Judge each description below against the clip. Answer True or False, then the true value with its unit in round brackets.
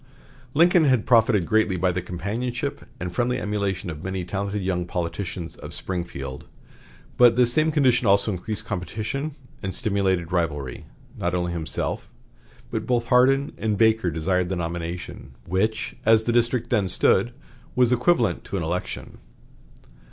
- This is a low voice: True (100 Hz)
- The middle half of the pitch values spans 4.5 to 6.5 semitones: True (5.2 semitones)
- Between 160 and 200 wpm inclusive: False (150 wpm)